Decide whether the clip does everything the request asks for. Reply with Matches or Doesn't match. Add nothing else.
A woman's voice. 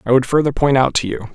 Doesn't match